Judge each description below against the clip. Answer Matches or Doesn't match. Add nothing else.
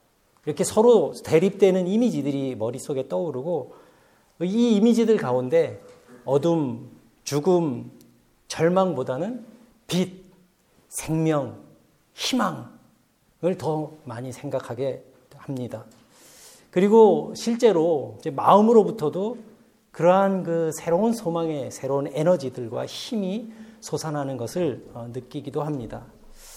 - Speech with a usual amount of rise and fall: Doesn't match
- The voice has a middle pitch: Matches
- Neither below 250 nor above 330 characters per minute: Doesn't match